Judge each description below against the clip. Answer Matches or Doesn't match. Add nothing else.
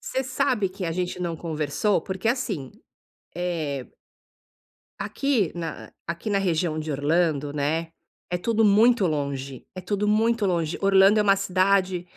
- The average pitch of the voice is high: Doesn't match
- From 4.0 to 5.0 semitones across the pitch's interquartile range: Matches